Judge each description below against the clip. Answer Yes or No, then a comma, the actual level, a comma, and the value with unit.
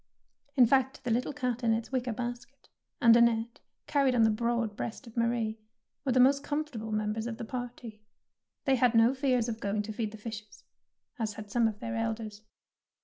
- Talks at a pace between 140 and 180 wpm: No, average, 195 wpm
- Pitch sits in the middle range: No, high, 235 Hz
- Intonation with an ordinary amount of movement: No, narrow, 2.2 semitones